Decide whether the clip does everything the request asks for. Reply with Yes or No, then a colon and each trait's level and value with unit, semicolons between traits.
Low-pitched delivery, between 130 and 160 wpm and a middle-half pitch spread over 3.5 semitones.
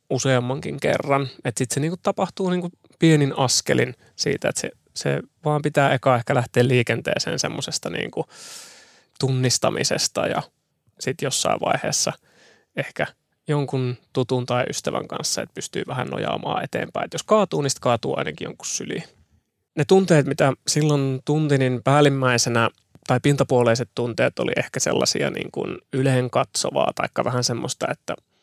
No: low, 130 Hz; average, 135 wpm; average, 2.9 semitones